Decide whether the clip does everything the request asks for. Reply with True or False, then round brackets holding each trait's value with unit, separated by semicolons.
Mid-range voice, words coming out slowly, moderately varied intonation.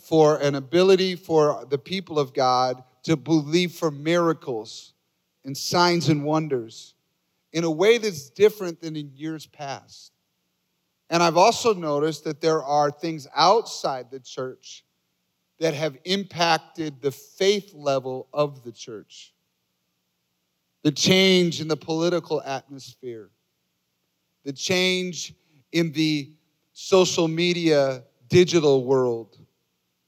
True (155 Hz; 120 wpm; 4.1 semitones)